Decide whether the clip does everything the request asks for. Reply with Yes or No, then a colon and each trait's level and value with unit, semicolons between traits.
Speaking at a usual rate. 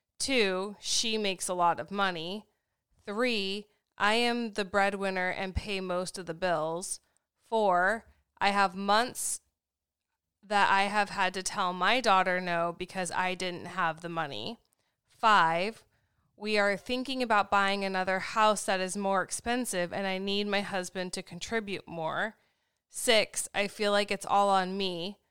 Yes: average, 155 wpm